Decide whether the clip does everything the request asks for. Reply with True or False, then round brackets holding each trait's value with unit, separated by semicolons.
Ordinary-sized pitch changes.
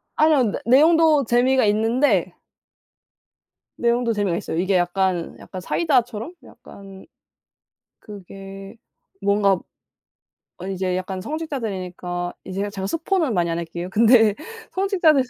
False (5.9 semitones)